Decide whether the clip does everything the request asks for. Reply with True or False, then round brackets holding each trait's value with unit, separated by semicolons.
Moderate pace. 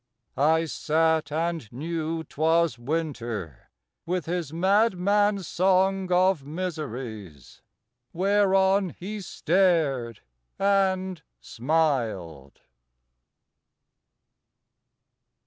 False (65 wpm)